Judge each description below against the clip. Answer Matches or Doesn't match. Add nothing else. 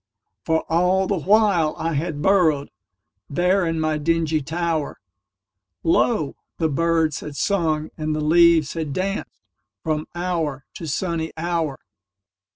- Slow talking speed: Matches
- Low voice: Doesn't match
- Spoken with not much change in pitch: Doesn't match